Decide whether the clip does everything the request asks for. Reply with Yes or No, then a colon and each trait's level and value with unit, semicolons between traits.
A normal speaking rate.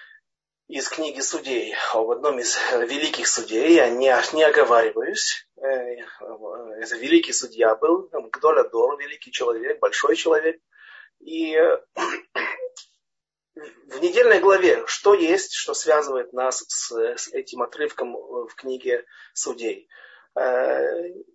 Yes: average, 125 wpm